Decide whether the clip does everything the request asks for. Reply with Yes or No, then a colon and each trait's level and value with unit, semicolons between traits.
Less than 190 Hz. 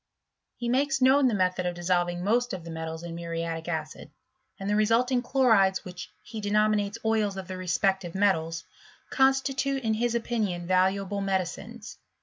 No: high, 200 Hz